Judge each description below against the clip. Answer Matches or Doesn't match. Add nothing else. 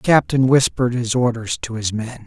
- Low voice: Matches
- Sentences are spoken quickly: Matches